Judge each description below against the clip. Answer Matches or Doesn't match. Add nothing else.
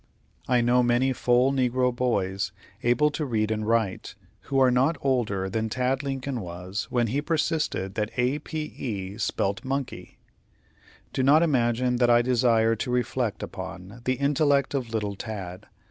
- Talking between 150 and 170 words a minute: Matches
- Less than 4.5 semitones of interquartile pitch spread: Matches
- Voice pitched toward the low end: Matches